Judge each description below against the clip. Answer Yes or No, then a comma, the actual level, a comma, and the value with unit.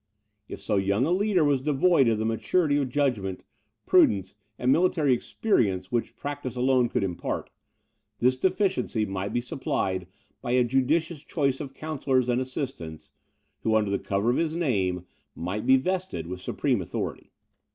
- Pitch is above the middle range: No, low, 130 Hz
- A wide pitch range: Yes, wide, 6.1 semitones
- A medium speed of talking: Yes, average, 160 wpm